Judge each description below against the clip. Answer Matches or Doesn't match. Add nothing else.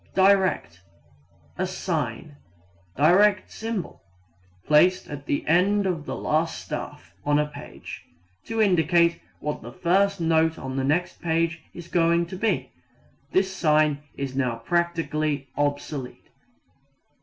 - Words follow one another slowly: Matches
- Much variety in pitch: Doesn't match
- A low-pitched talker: Doesn't match